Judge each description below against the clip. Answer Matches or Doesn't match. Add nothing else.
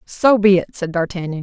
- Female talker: Matches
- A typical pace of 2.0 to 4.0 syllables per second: Doesn't match